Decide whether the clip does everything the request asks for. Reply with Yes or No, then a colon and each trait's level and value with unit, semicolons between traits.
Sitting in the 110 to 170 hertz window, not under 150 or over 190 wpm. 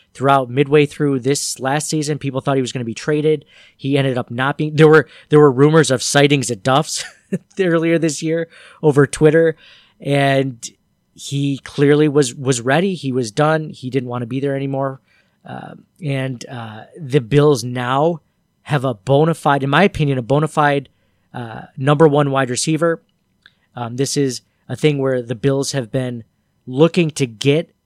Yes: medium, 140 Hz; average, 180 wpm